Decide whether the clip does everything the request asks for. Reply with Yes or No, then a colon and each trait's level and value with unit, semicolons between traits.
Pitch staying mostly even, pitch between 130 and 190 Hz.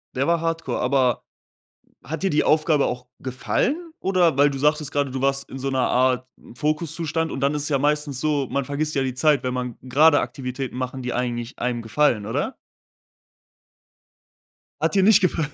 No: average, 3.3 semitones; medium, 140 Hz